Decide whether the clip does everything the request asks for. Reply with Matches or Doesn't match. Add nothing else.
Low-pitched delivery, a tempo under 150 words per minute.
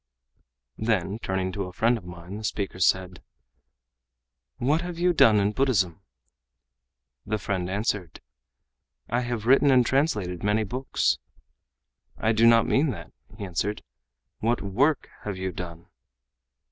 Matches